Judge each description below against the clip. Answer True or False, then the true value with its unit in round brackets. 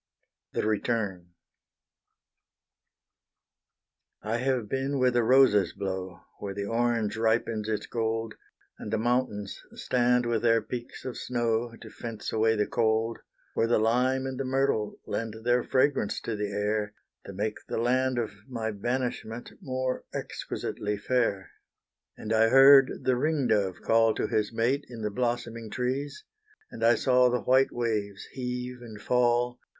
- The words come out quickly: False (150 wpm)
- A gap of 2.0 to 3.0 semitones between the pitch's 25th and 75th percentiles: True (2.6 semitones)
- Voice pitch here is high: False (115 Hz)